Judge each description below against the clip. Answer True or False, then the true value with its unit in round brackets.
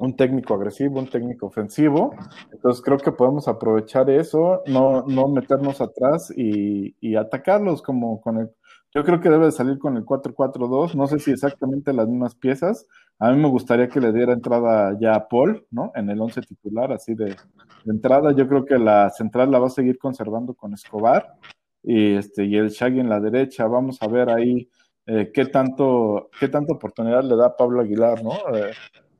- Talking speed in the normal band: False (195 wpm)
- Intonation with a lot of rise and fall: False (3.4 semitones)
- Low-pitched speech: True (125 Hz)